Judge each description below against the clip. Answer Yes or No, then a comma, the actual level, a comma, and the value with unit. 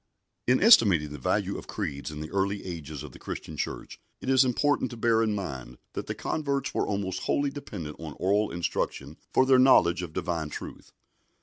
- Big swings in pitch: Yes, wide, 8.2 semitones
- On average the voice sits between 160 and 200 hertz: No, very low, 95 Hz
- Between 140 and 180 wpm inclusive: No, average, 195 wpm